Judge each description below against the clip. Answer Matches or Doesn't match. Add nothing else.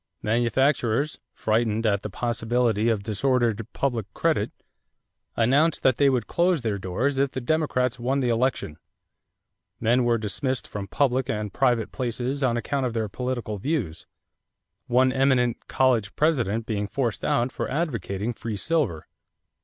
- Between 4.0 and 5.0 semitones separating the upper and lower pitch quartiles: Doesn't match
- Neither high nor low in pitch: Doesn't match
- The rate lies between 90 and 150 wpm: Matches